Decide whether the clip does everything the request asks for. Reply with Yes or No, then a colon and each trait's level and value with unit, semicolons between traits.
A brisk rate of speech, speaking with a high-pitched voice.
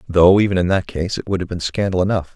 No: fast, 280 wpm; very low, 95 Hz